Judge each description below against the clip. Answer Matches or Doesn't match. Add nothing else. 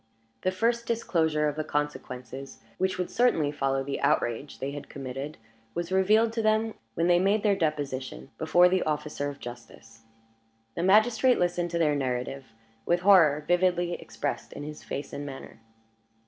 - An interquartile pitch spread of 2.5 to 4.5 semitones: Doesn't match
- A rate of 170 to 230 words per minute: Doesn't match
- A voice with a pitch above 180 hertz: Doesn't match